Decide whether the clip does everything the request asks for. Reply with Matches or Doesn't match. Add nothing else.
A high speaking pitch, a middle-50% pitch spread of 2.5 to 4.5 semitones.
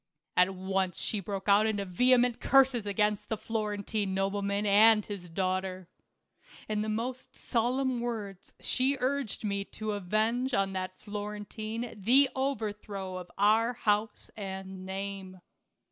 Matches